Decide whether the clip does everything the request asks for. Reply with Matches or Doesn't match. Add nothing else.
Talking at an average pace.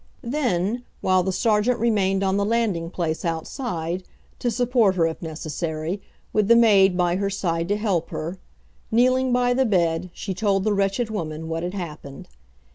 Matches